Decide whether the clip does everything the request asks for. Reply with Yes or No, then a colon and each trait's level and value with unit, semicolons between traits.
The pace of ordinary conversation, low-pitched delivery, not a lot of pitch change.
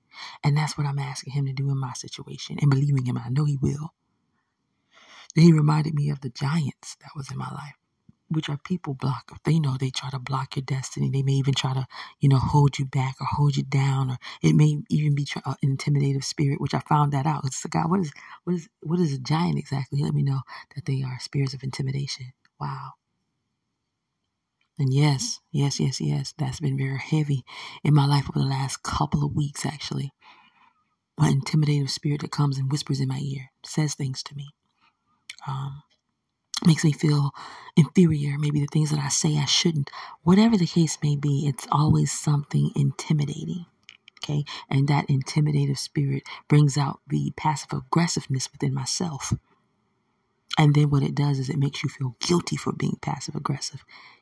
No: average, 190 wpm; medium, 145 Hz; narrow, 1.9 semitones